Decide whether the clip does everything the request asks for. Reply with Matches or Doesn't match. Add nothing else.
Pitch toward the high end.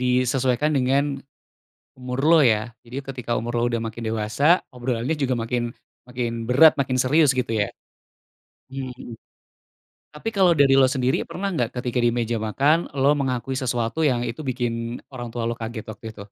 Doesn't match